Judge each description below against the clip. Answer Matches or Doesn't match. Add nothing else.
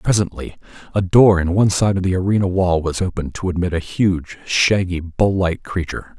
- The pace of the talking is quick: Doesn't match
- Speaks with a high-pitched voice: Doesn't match